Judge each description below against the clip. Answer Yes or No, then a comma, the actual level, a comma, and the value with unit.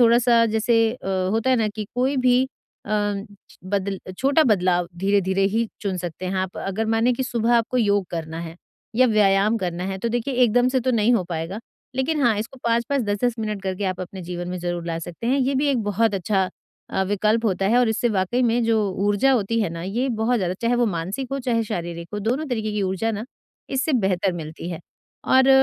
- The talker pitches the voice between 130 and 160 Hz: No, high, 215 Hz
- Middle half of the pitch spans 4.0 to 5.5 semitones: Yes, average, 4.4 semitones